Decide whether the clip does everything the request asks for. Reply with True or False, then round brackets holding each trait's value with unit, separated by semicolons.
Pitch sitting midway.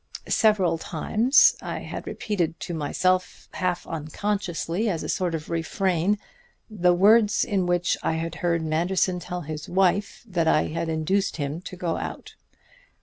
True (175 Hz)